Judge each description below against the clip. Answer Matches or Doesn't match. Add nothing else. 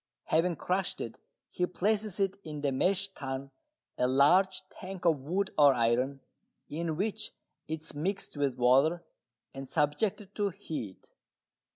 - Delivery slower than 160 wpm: Matches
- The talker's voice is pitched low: Doesn't match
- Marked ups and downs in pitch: Matches